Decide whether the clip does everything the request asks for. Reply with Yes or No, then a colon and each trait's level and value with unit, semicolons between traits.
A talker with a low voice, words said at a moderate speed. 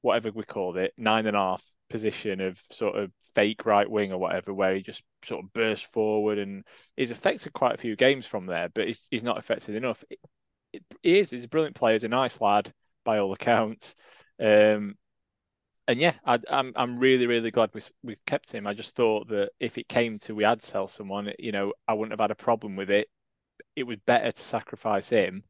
No: low, 105 Hz; fast, 220 wpm